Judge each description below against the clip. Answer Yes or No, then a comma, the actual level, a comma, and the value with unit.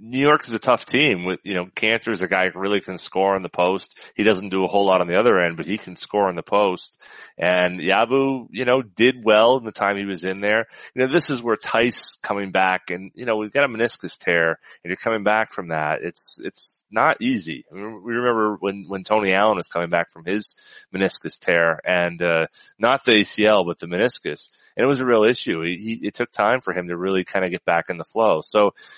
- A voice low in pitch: Yes, low, 100 Hz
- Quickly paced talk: Yes, fast, 255 wpm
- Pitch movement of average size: Yes, average, 3.6 semitones